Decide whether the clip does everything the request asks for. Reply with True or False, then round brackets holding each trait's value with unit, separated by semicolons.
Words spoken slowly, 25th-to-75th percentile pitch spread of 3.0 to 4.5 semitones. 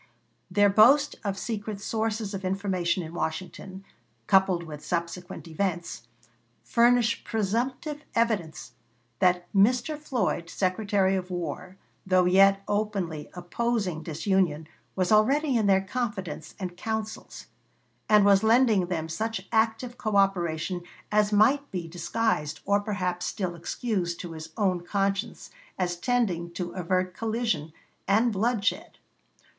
True (120 wpm; 3.8 semitones)